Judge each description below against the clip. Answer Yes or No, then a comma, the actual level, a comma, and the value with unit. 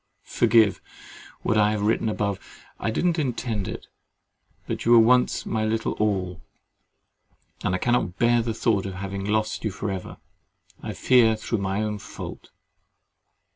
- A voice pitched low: Yes, low, 110 Hz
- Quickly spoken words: No, average, 160 wpm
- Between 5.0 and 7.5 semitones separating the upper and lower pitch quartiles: No, average, 2.7 semitones